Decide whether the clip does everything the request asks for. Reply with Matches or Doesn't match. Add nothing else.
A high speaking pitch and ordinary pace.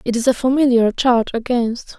Matches